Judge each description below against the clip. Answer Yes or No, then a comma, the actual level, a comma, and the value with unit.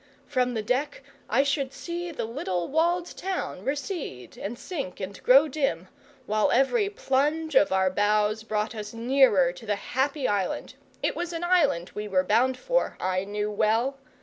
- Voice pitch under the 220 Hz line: No, very high, 250 Hz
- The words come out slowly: No, average, 170 wpm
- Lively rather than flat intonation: Yes, wide, 6.2 semitones